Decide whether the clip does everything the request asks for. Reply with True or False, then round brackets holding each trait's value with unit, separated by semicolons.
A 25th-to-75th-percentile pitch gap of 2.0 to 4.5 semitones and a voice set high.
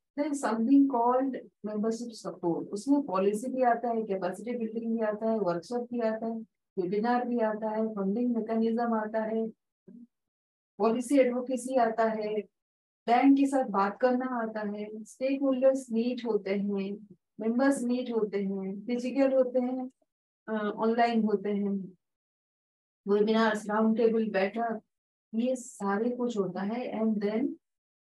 True (2.8 semitones; 225 Hz)